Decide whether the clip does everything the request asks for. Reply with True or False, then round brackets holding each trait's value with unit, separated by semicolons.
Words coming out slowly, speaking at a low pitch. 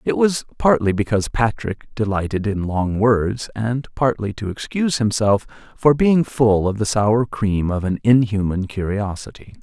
False (155 wpm; 110 Hz)